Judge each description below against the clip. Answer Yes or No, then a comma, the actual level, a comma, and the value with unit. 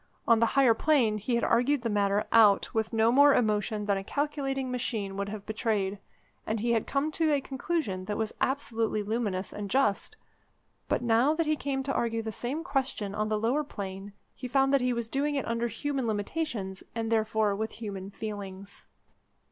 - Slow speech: No, average, 195 wpm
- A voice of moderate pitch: No, high, 225 Hz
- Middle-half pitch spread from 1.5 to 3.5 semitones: No, average, 4.5 semitones